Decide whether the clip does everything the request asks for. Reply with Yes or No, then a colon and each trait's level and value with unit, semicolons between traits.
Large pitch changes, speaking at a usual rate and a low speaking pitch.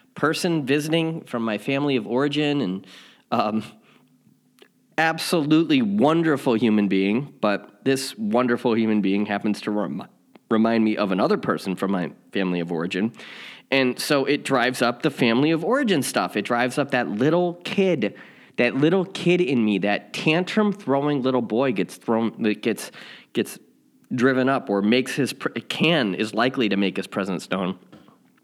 Yes: wide, 6.8 semitones; average, 160 wpm; low, 130 Hz